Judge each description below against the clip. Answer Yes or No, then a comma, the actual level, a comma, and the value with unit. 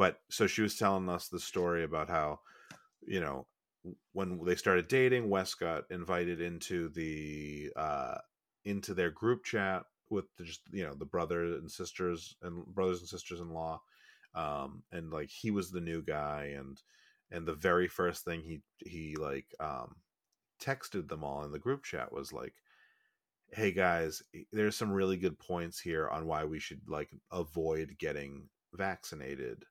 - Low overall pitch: Yes, very low, 85 Hz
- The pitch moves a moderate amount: Yes, average, 3.0 semitones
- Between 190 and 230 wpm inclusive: No, average, 170 wpm